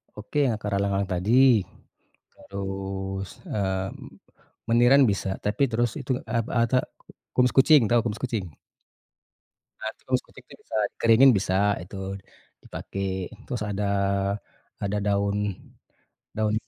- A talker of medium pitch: No, low, 105 Hz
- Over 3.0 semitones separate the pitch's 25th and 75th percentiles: Yes, average, 3.6 semitones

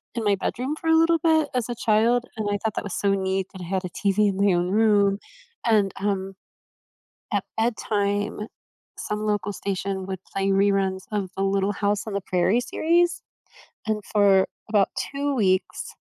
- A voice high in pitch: Yes, high, 205 Hz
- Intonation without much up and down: Yes, narrow, 2.3 semitones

